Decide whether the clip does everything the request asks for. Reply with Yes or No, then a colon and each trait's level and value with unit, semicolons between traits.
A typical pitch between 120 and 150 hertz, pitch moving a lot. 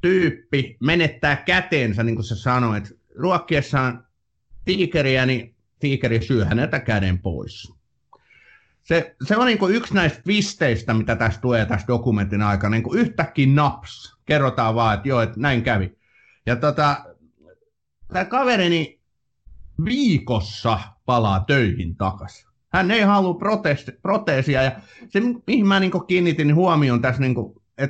Yes: low, 130 Hz; wide, 7.7 semitones